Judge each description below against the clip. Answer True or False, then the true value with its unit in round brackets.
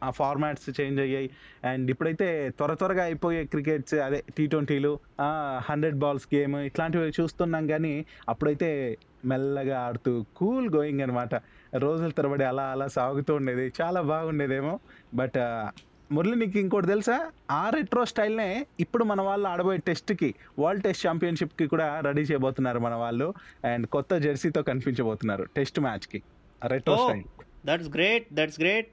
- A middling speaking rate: False (135 wpm)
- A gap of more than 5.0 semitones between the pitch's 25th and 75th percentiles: False (4.1 semitones)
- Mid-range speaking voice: True (150 Hz)